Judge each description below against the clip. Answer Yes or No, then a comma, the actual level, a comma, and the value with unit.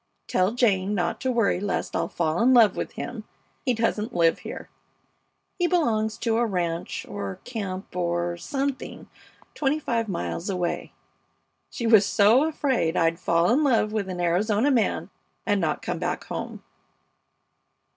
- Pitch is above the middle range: Yes, high, 210 Hz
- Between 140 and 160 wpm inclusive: Yes, average, 155 wpm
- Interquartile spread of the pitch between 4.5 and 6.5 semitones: Yes, wide, 5.4 semitones